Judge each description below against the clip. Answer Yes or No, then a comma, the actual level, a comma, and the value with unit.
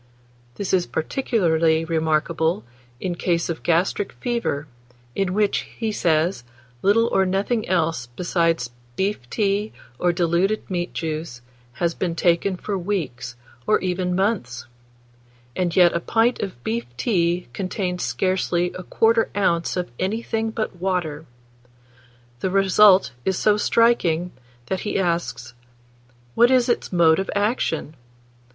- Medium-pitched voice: Yes, medium, 180 Hz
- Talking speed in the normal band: No, slow, 130 wpm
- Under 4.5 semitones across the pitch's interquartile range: Yes, average, 3.6 semitones